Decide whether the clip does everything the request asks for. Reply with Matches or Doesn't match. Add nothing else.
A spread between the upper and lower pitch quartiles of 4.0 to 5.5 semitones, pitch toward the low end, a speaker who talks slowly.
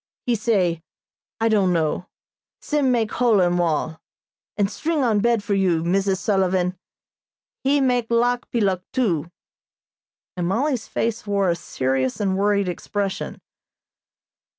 Doesn't match